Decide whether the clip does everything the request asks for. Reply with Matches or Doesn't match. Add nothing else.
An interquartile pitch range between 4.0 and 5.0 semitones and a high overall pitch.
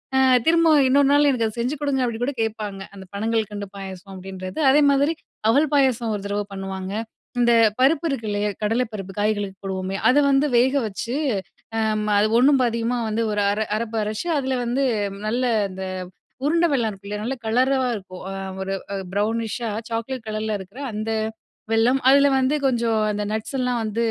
Matches